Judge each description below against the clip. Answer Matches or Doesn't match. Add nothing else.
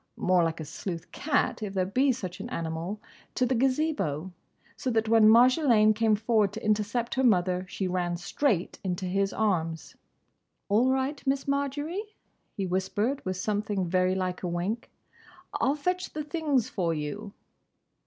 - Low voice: Doesn't match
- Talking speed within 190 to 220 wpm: Doesn't match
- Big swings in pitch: Matches